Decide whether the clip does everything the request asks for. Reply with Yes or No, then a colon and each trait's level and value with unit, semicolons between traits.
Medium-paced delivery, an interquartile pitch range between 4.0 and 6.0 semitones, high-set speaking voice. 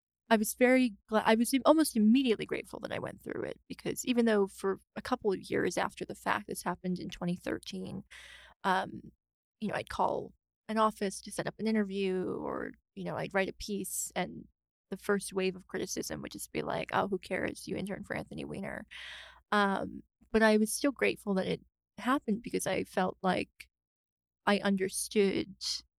No: average, 185 wpm; average, 2.8 semitones; high, 205 Hz